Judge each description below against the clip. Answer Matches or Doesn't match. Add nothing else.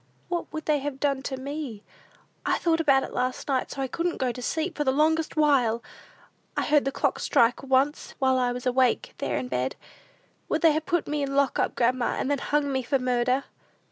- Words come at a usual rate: Doesn't match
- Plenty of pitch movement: Doesn't match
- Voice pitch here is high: Matches